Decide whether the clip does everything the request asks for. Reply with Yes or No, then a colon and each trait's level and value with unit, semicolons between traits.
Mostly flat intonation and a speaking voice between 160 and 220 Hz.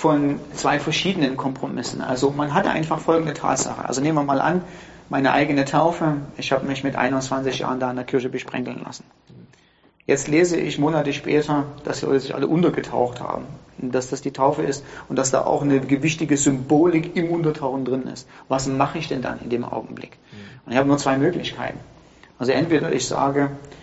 No: narrow, 2.2 semitones; medium, 140 Hz